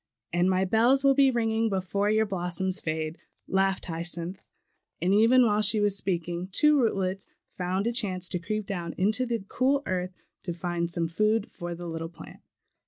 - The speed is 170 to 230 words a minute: Yes, average, 175 wpm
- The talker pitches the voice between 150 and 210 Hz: Yes, high, 190 Hz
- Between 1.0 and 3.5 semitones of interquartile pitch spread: No, average, 4.0 semitones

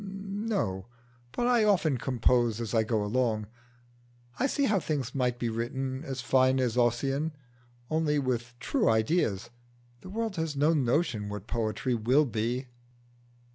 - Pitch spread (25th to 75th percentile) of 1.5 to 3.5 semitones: No, average, 5.3 semitones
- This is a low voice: Yes, low, 130 Hz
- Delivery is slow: No, average, 145 wpm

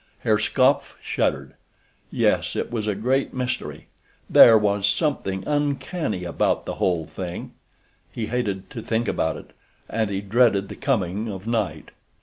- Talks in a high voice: No, low, 110 Hz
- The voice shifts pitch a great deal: No, average, 4.3 semitones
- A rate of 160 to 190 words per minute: No, slow, 135 wpm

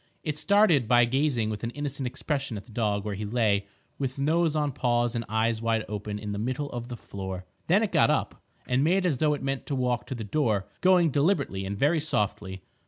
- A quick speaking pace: Yes, fast, 225 wpm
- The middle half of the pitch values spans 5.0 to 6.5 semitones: Yes, wide, 5.4 semitones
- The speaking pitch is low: Yes, low, 120 Hz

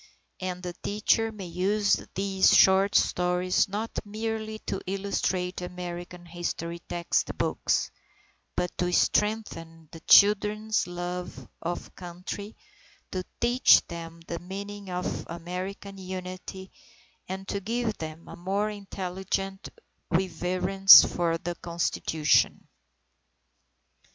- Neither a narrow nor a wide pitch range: No, narrow, 2.3 semitones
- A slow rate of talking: Yes, slow, 105 wpm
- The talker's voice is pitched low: No, medium, 185 Hz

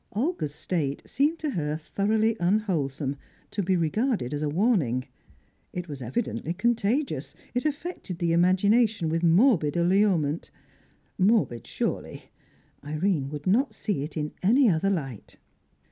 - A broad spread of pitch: Yes, wide, 6.4 semitones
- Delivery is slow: Yes, slow, 130 wpm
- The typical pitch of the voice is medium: Yes, medium, 180 Hz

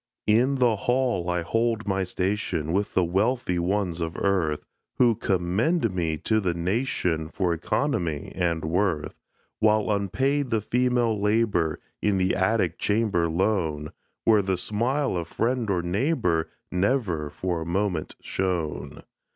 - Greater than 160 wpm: No, average, 140 wpm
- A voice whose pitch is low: Yes, very low, 95 Hz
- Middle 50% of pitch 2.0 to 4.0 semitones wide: No, average, 4.8 semitones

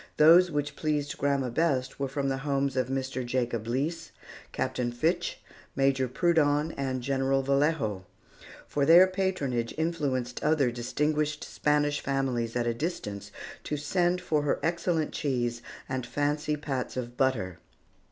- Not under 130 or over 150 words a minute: Yes, average, 140 wpm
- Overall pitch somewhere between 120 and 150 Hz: Yes, medium, 140 Hz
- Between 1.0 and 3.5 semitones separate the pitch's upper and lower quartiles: Yes, average, 3.1 semitones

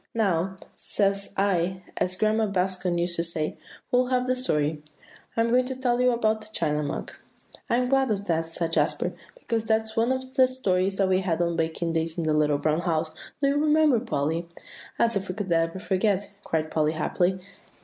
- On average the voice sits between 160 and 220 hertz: Yes, high, 190 Hz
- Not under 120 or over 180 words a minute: No, average, 200 wpm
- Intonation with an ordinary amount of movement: No, wide, 5.8 semitones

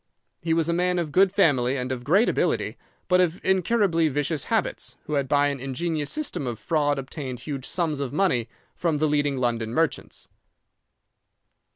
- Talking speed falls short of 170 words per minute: No, average, 175 wpm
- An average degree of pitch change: Yes, average, 4.3 semitones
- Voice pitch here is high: No, medium, 150 Hz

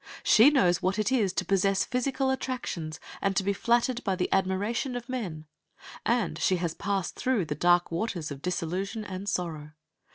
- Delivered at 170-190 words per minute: Yes, average, 175 wpm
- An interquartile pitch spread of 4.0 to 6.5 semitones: Yes, average, 5.1 semitones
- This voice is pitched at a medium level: No, high, 195 Hz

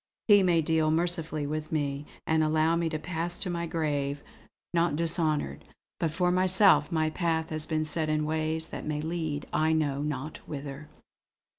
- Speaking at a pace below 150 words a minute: No, average, 170 wpm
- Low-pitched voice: No, medium, 155 Hz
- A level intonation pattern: Yes, narrow, 1.8 semitones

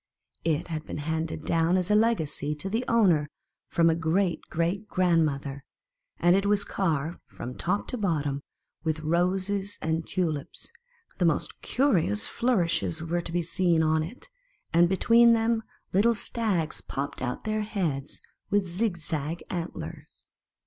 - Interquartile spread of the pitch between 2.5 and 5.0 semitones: Yes, average, 4.1 semitones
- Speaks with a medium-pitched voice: Yes, medium, 170 Hz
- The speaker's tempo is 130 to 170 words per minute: Yes, average, 160 wpm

